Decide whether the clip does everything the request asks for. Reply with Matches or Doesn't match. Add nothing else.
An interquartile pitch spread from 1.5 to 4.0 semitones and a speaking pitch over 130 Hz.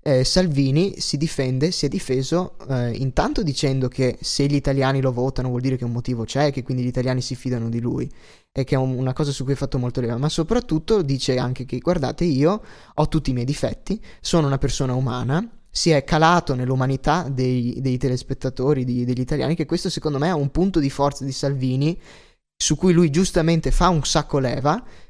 Matches